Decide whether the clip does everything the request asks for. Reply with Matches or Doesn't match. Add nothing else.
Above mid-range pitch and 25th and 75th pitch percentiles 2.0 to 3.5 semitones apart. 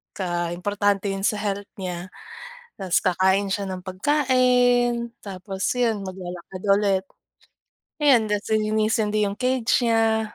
Matches